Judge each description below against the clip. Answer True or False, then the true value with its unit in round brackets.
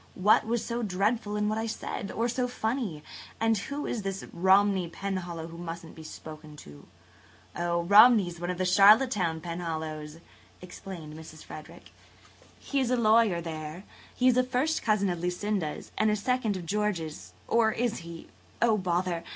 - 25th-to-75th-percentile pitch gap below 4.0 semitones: False (4.7 semitones)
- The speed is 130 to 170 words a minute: True (165 wpm)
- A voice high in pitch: True (195 Hz)